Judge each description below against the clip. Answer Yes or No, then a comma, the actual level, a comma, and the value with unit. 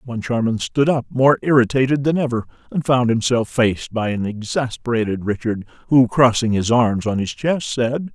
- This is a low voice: Yes, low, 120 Hz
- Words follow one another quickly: No, average, 170 wpm